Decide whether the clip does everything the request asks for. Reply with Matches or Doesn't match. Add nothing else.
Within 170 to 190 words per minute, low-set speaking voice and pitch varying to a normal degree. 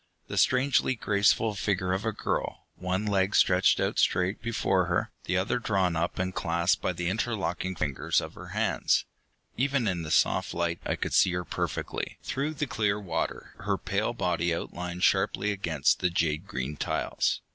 Matches